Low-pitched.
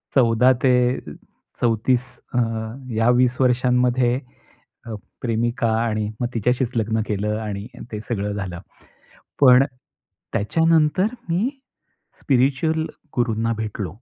Yes: low, 120 Hz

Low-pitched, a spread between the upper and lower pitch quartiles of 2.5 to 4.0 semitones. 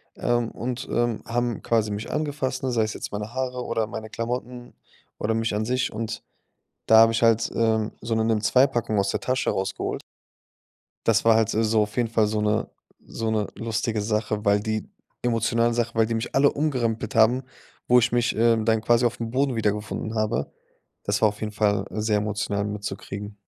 No: low, 115 Hz; narrow, 2.0 semitones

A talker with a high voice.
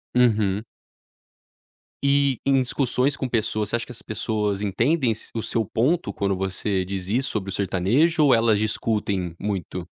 No: low, 110 Hz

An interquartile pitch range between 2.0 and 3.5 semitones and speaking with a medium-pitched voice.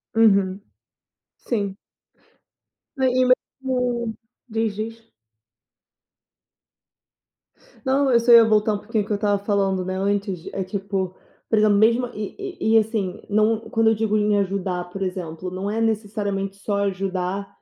No: narrow, 2.4 semitones; high, 205 Hz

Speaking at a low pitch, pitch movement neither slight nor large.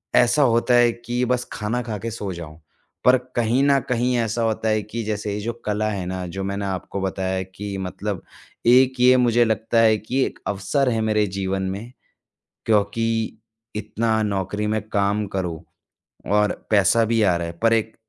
Yes: low, 110 Hz; average, 3.1 semitones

